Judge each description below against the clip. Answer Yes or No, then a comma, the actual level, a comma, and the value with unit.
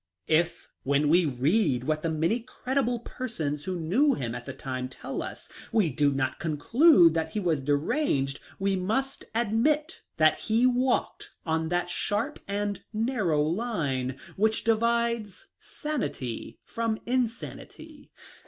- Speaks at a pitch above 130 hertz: Yes, high, 190 Hz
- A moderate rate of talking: Yes, average, 145 wpm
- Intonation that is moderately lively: No, wide, 7.7 semitones